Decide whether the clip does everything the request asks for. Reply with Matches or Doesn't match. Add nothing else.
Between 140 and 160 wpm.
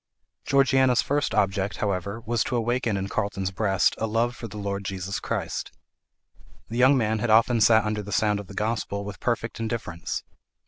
Doesn't match